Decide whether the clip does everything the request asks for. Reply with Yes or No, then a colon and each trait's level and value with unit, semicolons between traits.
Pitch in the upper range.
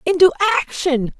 Yes: very high, 320 Hz